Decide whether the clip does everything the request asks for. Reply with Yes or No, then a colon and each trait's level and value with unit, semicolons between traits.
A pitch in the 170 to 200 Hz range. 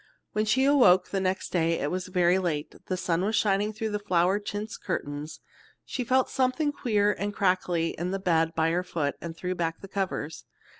Yes: medium, 185 Hz